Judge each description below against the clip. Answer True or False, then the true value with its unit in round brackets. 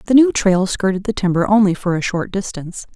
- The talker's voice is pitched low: False (195 Hz)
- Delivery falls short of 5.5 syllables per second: False (5.9 syllables/s)